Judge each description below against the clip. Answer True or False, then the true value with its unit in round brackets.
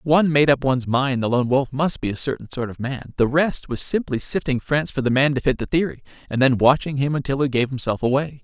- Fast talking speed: True (265 wpm)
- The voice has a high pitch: False (135 Hz)